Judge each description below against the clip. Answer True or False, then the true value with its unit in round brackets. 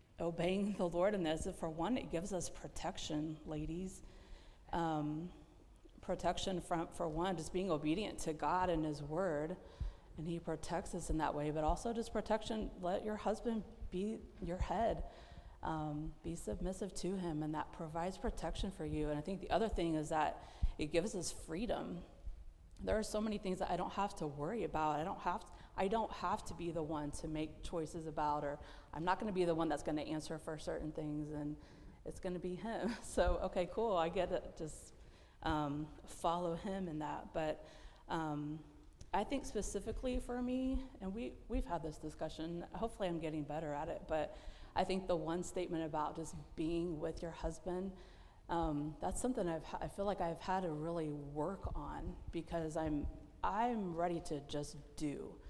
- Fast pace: False (185 wpm)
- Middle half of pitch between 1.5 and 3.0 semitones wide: False (3.5 semitones)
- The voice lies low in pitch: False (170 Hz)